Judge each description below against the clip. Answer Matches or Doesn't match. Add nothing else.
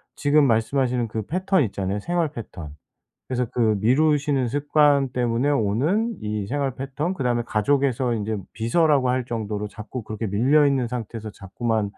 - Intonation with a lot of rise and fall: Doesn't match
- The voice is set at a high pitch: Doesn't match